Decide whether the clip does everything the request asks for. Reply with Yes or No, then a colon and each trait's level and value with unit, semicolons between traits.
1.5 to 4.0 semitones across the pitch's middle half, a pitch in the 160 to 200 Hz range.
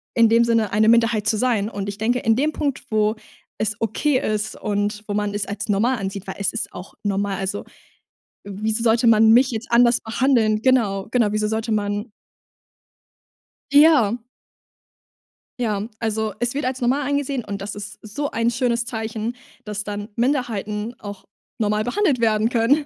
No: narrow, 2.6 semitones; high, 220 Hz